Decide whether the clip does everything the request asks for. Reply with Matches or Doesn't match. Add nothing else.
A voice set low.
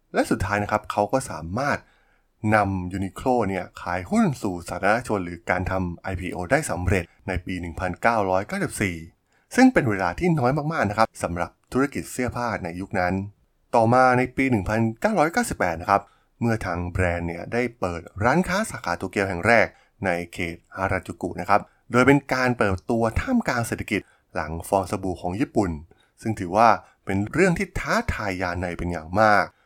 Matches